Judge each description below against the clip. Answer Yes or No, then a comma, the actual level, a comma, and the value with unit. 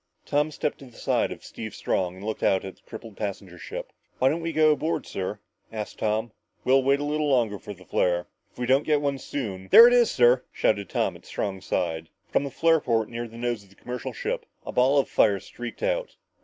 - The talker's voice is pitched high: No, low, 120 Hz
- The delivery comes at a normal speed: No, fast, 235 wpm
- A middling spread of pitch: No, wide, 6.1 semitones